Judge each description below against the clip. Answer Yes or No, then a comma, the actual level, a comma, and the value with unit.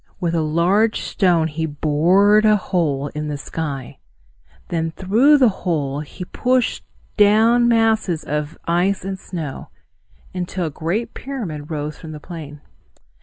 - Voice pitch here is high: No, medium, 170 Hz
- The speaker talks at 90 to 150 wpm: Yes, average, 140 wpm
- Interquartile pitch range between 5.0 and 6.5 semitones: Yes, wide, 5.4 semitones